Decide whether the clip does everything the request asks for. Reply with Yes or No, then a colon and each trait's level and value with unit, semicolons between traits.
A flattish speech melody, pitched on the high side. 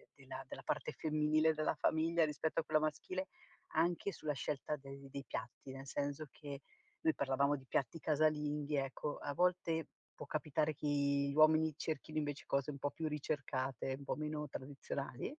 No: narrow, 2.0 semitones; medium, 150 Hz